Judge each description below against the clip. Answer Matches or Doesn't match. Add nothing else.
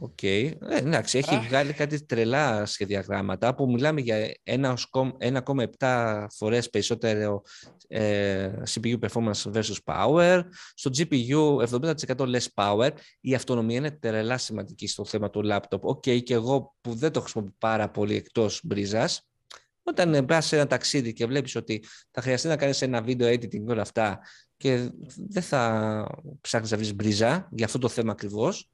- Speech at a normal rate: Matches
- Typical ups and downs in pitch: Matches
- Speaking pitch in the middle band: Doesn't match